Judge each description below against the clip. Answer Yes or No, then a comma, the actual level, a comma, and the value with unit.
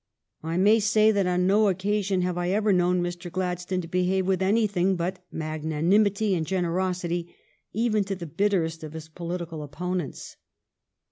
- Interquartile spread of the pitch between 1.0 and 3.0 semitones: Yes, narrow, 2.4 semitones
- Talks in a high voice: No, medium, 180 Hz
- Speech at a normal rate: Yes, average, 165 wpm